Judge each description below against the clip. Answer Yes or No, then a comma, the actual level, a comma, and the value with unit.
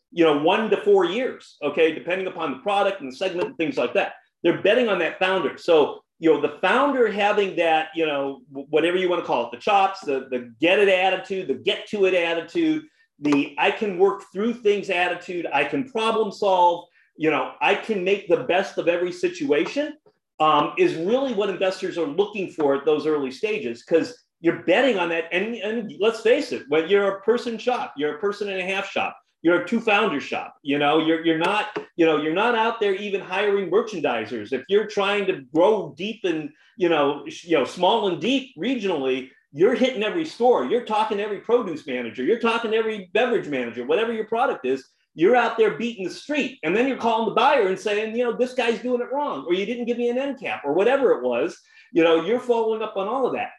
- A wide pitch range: Yes, wide, 5.9 semitones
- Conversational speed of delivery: No, fast, 225 wpm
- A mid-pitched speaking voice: No, high, 200 Hz